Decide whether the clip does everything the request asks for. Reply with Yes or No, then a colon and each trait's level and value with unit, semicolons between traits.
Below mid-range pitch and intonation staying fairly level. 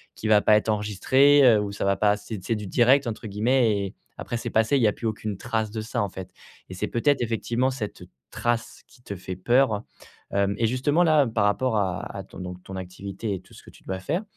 No: low, 110 Hz; average, 3.3 semitones